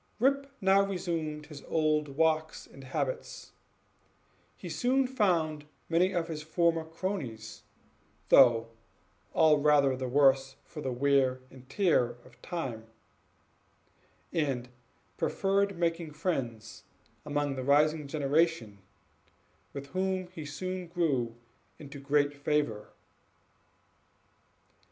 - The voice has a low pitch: No, medium, 150 Hz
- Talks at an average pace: No, slow, 105 wpm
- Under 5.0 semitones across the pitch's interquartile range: Yes, average, 4.1 semitones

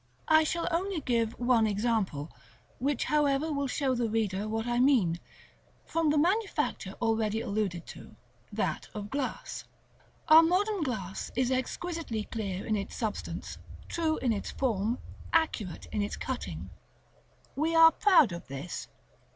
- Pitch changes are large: Yes, wide, 6.7 semitones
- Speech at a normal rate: Yes, average, 150 wpm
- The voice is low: No, high, 245 Hz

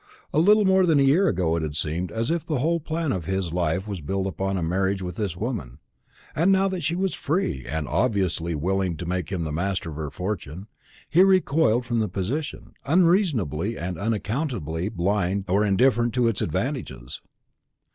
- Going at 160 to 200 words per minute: Yes, average, 190 wpm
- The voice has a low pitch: Yes, low, 100 Hz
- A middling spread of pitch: No, wide, 8.7 semitones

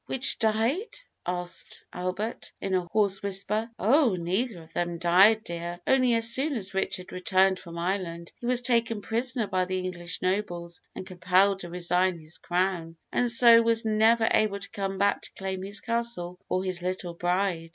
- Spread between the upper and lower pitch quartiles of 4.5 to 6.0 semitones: No, average, 4.0 semitones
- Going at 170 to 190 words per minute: Yes, average, 175 wpm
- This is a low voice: No, high, 190 Hz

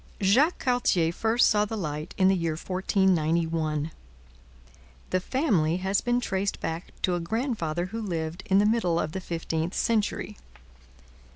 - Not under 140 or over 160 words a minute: Yes, average, 150 wpm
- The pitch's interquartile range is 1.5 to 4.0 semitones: No, average, 4.6 semitones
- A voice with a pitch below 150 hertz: No, medium, 185 Hz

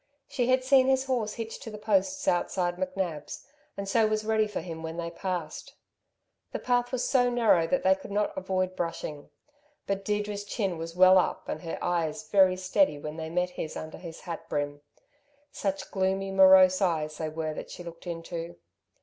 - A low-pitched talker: No, medium, 185 Hz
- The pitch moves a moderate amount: Yes, average, 4.0 semitones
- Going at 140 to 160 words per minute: No, average, 190 wpm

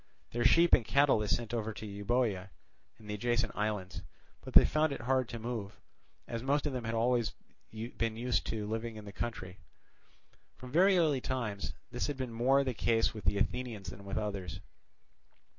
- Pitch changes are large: No, average, 3.2 semitones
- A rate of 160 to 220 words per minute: Yes, average, 190 wpm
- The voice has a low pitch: Yes, low, 115 Hz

